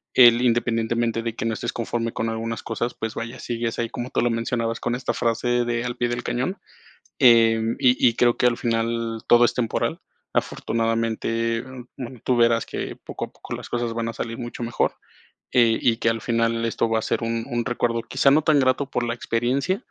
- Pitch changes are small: Yes, narrow, 1.0 semitones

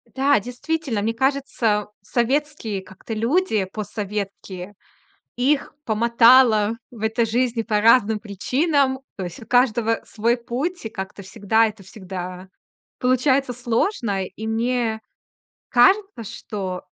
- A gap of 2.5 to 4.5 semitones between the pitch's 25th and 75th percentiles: Yes, average, 3.5 semitones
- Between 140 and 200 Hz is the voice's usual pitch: No, high, 230 Hz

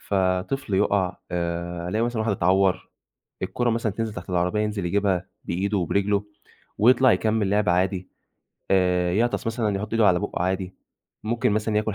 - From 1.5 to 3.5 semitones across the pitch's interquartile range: Yes, average, 3.0 semitones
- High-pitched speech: No, low, 100 Hz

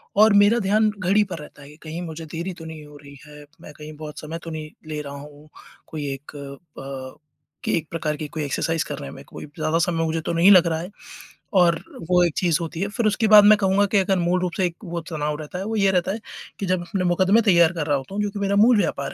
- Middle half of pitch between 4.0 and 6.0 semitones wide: Yes, average, 4.3 semitones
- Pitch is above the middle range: No, medium, 170 Hz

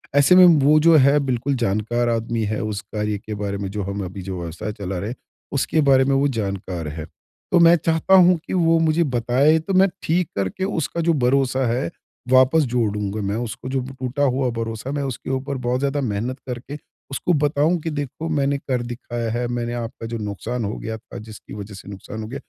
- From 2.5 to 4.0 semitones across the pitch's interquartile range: No, average, 5.0 semitones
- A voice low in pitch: Yes, low, 125 Hz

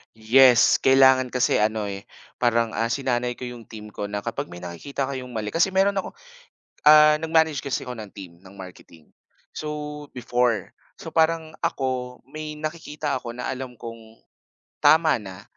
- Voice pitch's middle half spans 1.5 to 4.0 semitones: No, average, 5.2 semitones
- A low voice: Yes, low, 125 Hz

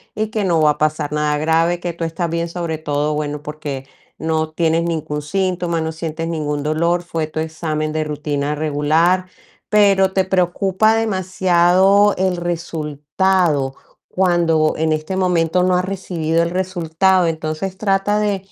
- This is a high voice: No, medium, 165 Hz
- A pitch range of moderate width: Yes, average, 3.1 semitones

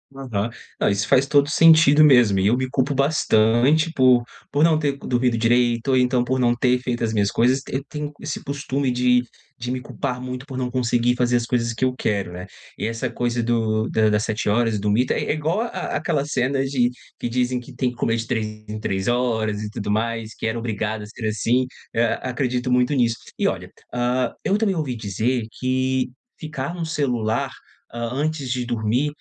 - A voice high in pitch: No, low, 125 Hz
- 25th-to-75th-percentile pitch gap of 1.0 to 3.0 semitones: Yes, average, 2.7 semitones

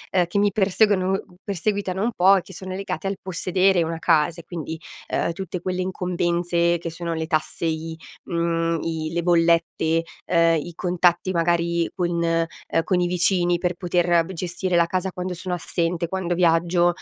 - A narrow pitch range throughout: Yes, narrow, 1.7 semitones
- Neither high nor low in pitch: Yes, medium, 175 Hz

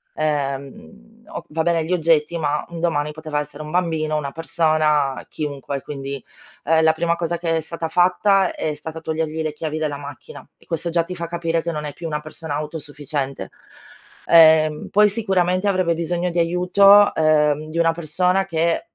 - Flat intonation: Yes, narrow, 2.2 semitones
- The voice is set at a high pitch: No, medium, 160 Hz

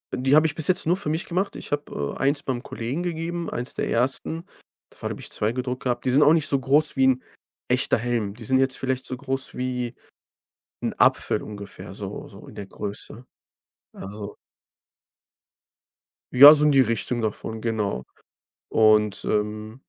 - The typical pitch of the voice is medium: No, low, 130 Hz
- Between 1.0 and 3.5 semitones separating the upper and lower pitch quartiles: No, average, 4.7 semitones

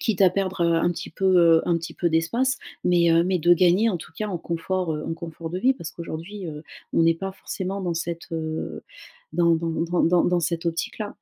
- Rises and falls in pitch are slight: Yes, narrow, 2.2 semitones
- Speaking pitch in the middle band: Yes, medium, 170 Hz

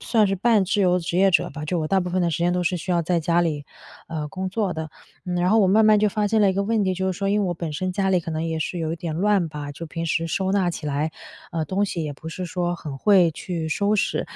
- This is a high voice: No, medium, 180 Hz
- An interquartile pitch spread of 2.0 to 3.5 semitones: Yes, average, 3.1 semitones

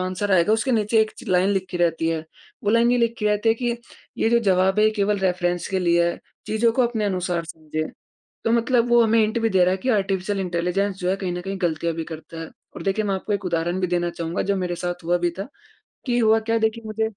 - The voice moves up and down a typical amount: Yes, average, 3.8 semitones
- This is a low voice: No, high, 190 Hz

